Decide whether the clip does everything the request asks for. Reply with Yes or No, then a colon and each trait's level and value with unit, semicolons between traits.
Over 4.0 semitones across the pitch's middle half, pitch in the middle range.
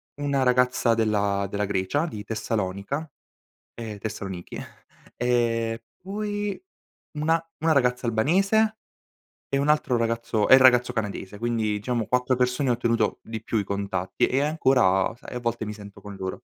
No: average, 4.7 semitones; low, 115 Hz